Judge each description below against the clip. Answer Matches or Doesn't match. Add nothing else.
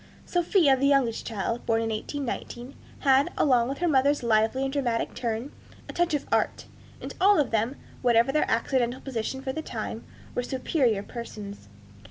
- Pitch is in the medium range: Doesn't match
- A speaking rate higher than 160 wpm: Matches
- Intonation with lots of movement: Doesn't match